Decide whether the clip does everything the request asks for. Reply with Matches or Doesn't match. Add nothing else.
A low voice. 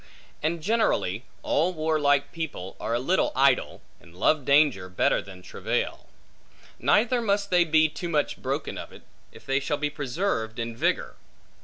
Doesn't match